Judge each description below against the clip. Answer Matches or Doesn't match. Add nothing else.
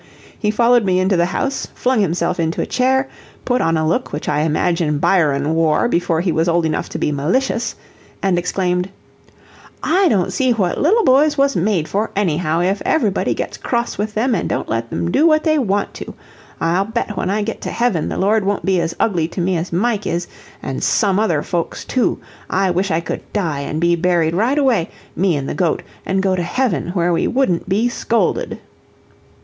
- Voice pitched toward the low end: Doesn't match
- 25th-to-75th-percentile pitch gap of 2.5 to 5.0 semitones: Doesn't match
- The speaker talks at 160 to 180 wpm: Doesn't match